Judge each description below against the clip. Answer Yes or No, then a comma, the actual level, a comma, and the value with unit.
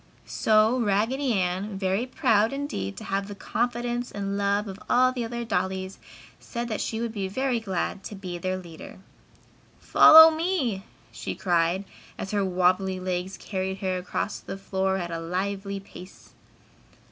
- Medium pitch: No, high, 200 Hz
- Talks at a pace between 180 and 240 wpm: No, average, 160 wpm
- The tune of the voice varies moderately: Yes, average, 3.8 semitones